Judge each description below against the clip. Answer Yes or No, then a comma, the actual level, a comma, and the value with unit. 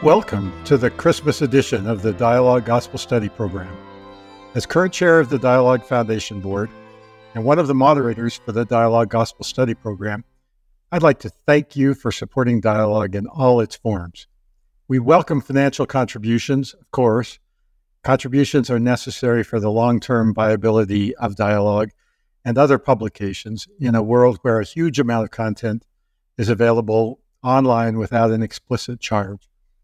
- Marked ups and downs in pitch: No, average, 3.6 semitones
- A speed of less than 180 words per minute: Yes, average, 155 wpm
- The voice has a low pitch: Yes, low, 115 Hz